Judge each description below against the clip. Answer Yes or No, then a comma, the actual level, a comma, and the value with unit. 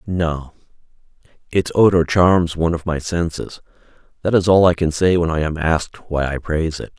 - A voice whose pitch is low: Yes, very low, 85 Hz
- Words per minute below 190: Yes, average, 180 wpm